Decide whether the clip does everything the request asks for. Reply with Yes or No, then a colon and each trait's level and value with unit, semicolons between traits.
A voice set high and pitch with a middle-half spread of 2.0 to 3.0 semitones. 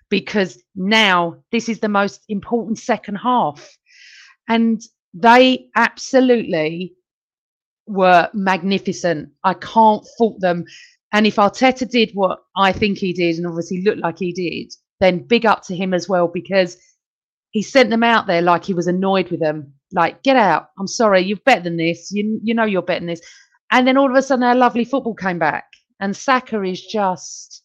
No: high, 195 Hz; average, 4.3 semitones